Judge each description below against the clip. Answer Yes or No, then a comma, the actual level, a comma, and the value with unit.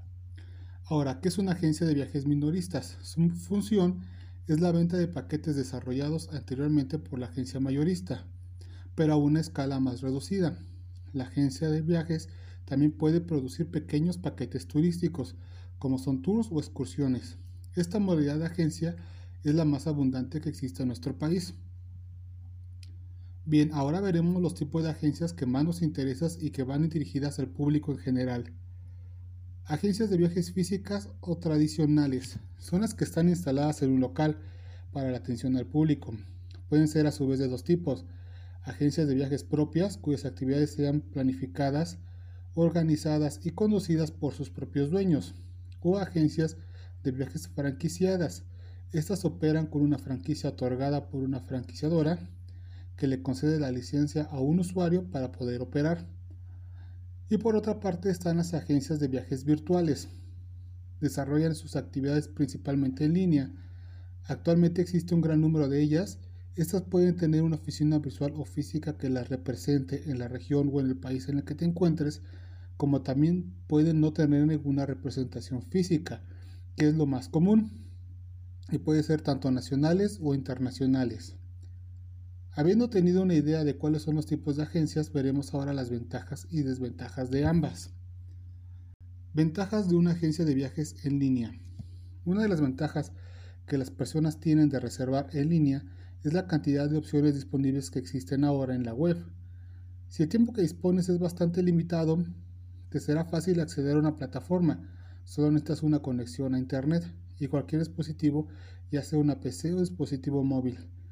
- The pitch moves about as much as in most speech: No, wide, 8.2 semitones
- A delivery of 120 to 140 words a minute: No, average, 155 wpm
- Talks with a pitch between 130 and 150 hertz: Yes, medium, 140 Hz